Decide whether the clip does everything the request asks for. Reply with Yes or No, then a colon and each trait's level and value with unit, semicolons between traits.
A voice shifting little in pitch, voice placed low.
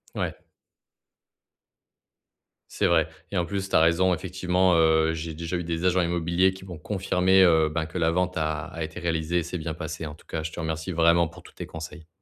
Yes: narrow, 2.1 semitones; very low, 85 Hz